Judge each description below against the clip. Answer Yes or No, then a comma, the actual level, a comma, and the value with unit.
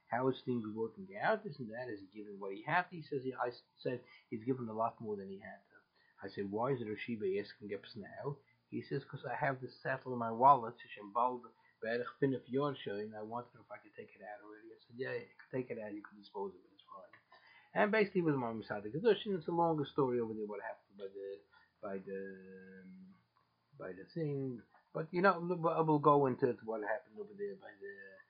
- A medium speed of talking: No, fast, 235 wpm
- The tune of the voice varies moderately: No, wide, 6.1 semitones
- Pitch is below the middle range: Yes, low, 125 Hz